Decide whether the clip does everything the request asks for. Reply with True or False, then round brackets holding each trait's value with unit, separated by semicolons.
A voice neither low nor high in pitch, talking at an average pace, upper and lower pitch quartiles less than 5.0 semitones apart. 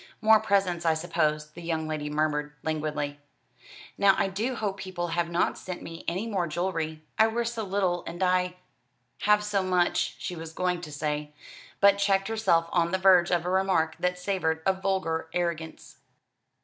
True (175 Hz; 180 wpm; 3.2 semitones)